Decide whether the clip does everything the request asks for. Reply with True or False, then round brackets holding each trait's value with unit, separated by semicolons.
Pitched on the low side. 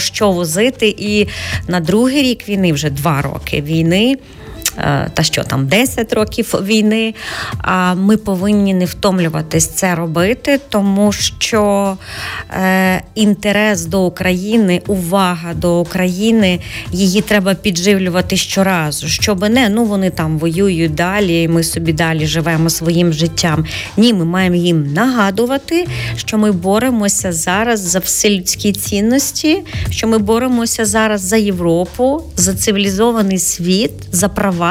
False (195 Hz)